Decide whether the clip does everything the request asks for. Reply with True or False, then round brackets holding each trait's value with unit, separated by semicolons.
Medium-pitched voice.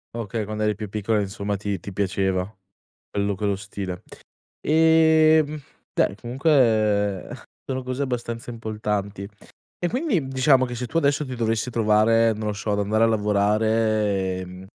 False (110 Hz)